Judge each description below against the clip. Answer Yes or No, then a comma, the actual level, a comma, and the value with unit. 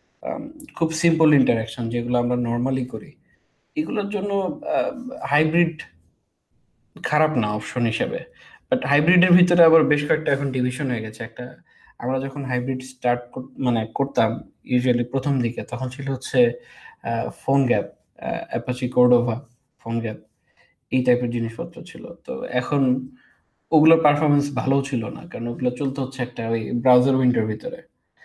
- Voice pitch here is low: Yes, low, 130 Hz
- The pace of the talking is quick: Yes, fast, 130 wpm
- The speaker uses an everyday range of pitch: Yes, average, 4.4 semitones